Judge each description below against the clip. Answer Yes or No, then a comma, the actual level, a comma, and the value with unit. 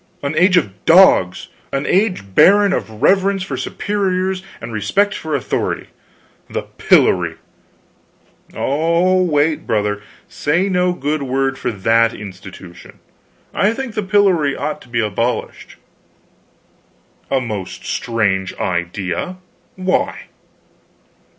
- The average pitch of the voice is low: No, medium, 150 Hz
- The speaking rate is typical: No, slow, 115 wpm